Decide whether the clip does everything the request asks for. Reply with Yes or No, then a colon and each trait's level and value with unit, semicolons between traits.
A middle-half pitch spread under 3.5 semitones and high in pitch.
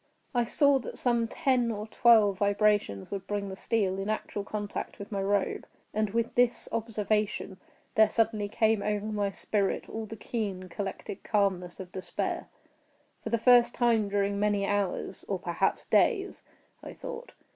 Yes: narrow, 2.4 semitones; high, 210 Hz